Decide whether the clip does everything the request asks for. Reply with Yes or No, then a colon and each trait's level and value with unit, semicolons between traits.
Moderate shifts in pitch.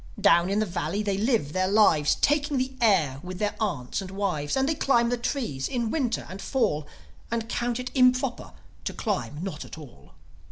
No: wide, 6.1 semitones